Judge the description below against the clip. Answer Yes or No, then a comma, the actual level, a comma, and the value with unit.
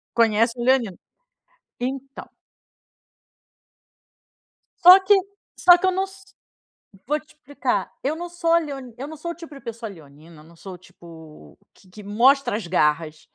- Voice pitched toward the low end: No, very high, 250 Hz